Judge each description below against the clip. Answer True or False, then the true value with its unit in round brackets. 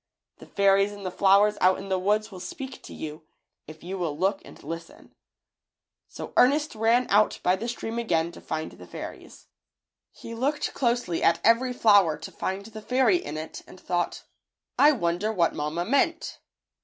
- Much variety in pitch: False (5.0 semitones)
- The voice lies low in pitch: False (200 Hz)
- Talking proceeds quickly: False (180 wpm)